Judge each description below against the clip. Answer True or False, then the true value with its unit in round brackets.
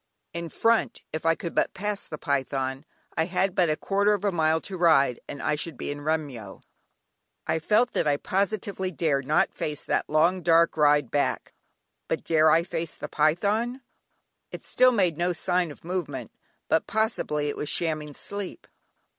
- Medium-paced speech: True (180 wpm)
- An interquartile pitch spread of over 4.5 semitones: False (4.0 semitones)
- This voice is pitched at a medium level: True (165 Hz)